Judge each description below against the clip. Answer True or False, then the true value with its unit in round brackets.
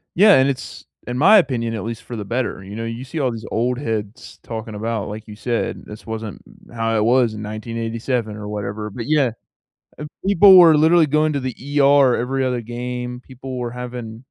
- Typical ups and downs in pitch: True (3.0 semitones)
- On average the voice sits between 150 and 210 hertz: False (120 Hz)